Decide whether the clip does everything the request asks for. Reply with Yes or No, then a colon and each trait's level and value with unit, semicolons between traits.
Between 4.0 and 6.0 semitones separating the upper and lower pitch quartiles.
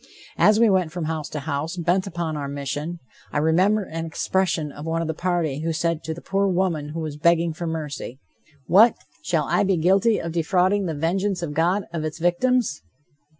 No: average, 3.1 semitones